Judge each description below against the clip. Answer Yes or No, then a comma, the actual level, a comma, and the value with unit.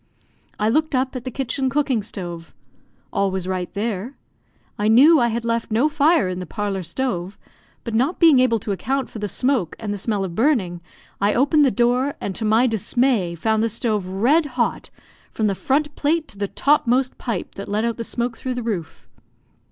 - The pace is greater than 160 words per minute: Yes, average, 200 wpm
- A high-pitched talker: Yes, high, 230 Hz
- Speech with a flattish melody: No, average, 4.7 semitones